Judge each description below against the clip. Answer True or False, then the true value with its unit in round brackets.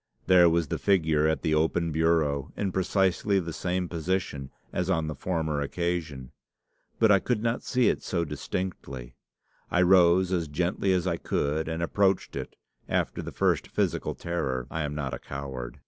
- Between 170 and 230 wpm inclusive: True (175 wpm)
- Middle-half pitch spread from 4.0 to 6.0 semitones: False (3.5 semitones)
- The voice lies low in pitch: True (85 Hz)